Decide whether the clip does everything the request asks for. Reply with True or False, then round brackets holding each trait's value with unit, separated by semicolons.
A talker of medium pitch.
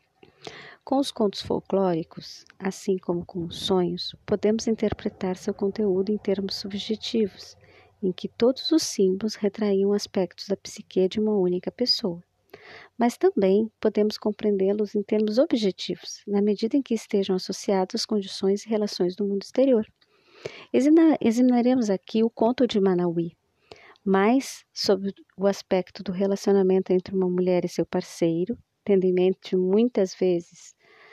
False (200 Hz)